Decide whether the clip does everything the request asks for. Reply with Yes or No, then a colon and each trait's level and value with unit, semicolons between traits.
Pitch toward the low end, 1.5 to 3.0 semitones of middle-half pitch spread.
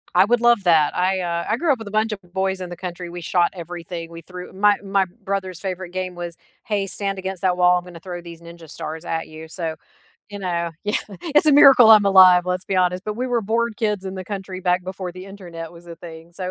No: medium, 185 Hz; narrow, 2.4 semitones